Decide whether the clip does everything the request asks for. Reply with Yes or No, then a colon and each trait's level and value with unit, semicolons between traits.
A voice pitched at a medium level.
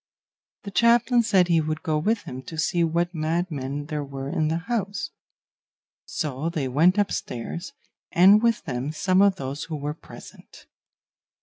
Yes: medium, 165 Hz